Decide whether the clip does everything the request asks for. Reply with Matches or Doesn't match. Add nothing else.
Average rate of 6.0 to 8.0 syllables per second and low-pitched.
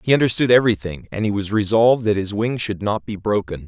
Matches